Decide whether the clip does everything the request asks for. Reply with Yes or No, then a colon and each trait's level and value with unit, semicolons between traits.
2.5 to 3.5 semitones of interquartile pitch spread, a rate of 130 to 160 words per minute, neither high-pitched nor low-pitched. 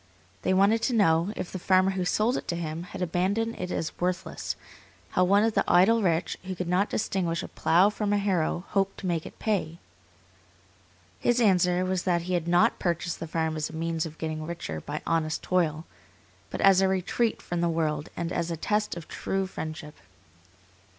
No: average, 2.8 semitones; average, 200 wpm; medium, 180 Hz